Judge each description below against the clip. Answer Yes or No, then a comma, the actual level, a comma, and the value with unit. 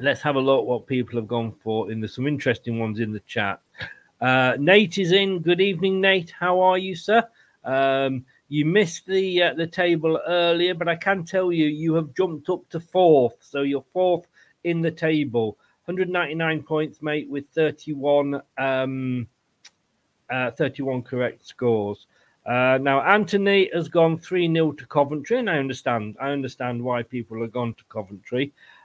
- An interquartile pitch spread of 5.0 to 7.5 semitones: Yes, wide, 5.6 semitones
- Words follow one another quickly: No, average, 175 wpm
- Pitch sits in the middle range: Yes, medium, 150 Hz